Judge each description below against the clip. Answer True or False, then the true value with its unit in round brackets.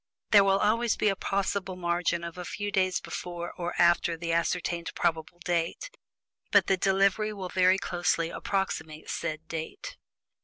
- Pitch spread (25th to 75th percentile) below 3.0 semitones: True (2.5 semitones)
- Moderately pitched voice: True (180 Hz)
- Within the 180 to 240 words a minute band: False (155 wpm)